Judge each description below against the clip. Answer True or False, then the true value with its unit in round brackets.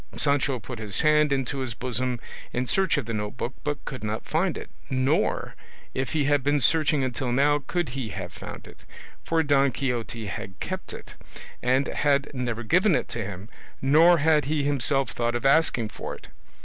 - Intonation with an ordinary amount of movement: True (3.6 semitones)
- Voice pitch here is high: False (135 Hz)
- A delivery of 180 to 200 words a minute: True (190 wpm)